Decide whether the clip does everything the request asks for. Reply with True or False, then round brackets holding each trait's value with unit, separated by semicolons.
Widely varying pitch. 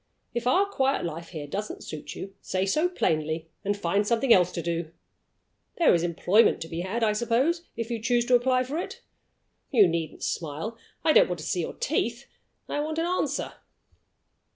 True (7.2 semitones)